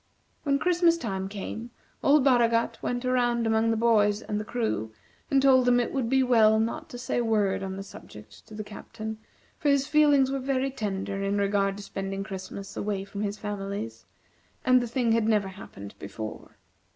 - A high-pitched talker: Yes, high, 220 Hz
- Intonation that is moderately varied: Yes, average, 4.1 semitones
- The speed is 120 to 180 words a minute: No, average, 190 wpm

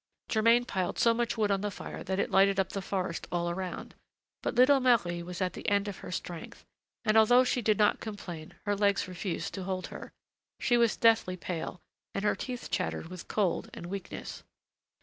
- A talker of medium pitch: No, high, 195 Hz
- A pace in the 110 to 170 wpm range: No, average, 200 wpm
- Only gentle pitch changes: No, average, 3.4 semitones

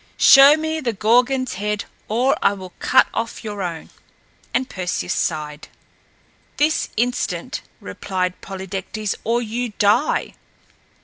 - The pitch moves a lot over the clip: No, average, 4.6 semitones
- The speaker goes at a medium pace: No, slow, 120 wpm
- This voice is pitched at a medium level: No, high, 215 Hz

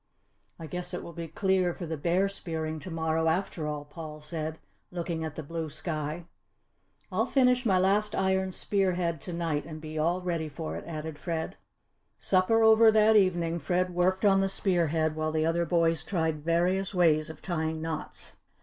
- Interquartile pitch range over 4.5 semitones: No, average, 2.8 semitones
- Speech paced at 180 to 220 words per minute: Yes, average, 185 wpm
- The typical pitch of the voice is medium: Yes, medium, 170 Hz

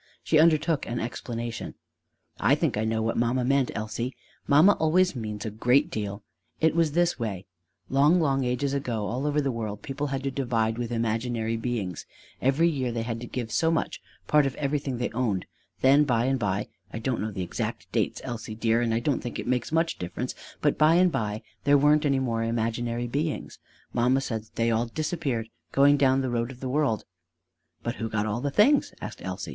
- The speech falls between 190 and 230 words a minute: Yes, fast, 205 wpm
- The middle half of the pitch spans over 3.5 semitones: Yes, average, 4.0 semitones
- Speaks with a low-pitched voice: Yes, low, 125 Hz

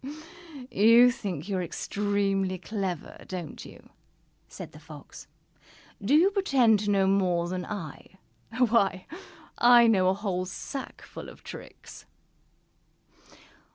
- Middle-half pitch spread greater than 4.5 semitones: No, average, 3.8 semitones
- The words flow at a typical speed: No, slow, 120 wpm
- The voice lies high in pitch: Yes, high, 195 Hz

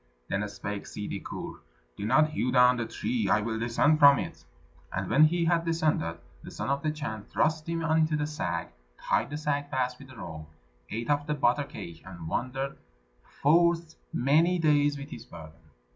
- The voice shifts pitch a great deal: Yes, wide, 5.9 semitones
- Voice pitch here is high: No, medium, 140 Hz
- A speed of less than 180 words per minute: No, average, 190 wpm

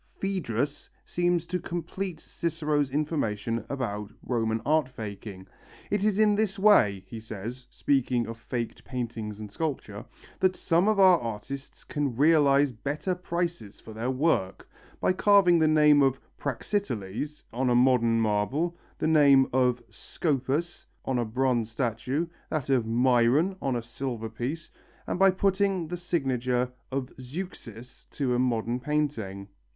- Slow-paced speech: No, average, 145 wpm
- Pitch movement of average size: No, wide, 6.1 semitones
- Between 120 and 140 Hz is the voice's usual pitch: Yes, low, 135 Hz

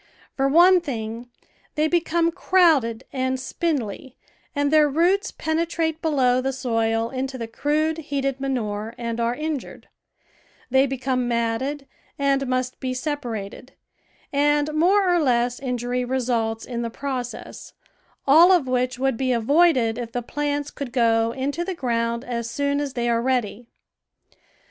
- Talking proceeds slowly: No, average, 145 wpm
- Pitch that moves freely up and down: No, average, 3.7 semitones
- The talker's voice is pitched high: Yes, very high, 260 Hz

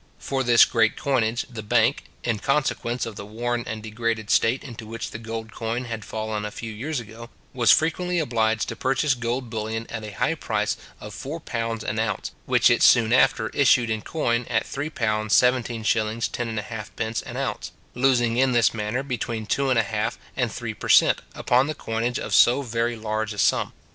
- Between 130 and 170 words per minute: No, average, 190 wpm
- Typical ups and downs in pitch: No, narrow, 2.2 semitones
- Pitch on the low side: Yes, low, 115 Hz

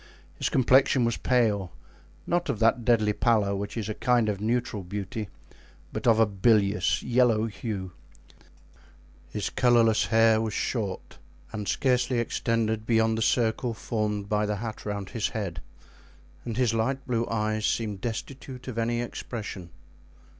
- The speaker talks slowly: No, average, 145 wpm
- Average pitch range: No, narrow, 2.2 semitones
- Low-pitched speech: Yes, low, 110 Hz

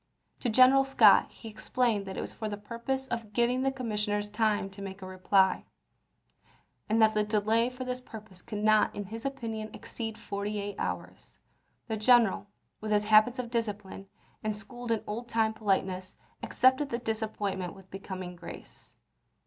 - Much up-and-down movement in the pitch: No, narrow, 2.6 semitones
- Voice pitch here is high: Yes, high, 215 Hz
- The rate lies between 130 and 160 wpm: No, average, 170 wpm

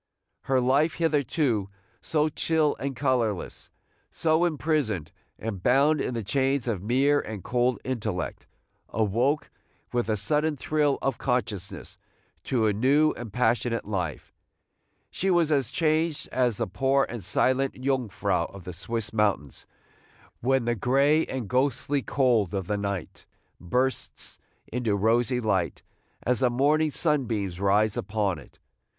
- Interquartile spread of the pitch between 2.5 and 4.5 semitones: No, average, 4.9 semitones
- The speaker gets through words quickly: No, slow, 135 wpm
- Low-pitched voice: Yes, low, 125 Hz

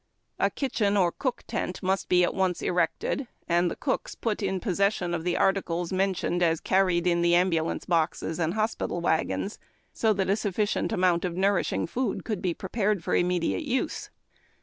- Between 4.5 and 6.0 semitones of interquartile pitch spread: No, average, 2.7 semitones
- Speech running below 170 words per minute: No, average, 175 wpm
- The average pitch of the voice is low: No, medium, 185 Hz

